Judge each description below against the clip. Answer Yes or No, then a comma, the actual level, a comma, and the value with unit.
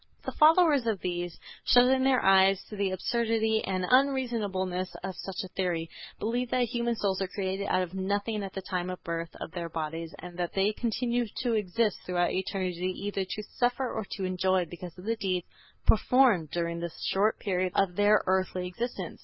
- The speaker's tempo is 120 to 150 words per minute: No, average, 190 wpm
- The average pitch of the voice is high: Yes, high, 195 Hz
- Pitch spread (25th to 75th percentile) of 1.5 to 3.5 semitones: No, average, 4.0 semitones